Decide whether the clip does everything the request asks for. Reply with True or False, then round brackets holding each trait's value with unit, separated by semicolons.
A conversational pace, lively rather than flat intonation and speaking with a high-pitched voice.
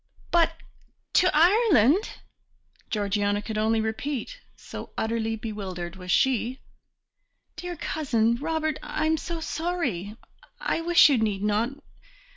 False (115 wpm; 7.2 semitones; 240 Hz)